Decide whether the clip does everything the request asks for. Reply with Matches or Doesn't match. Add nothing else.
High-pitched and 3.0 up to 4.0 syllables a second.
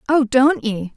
Matches